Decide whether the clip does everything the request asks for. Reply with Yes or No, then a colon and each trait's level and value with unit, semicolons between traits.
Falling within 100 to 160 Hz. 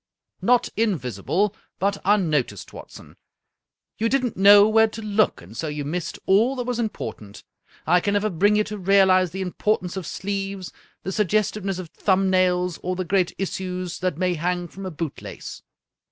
No: high, 190 Hz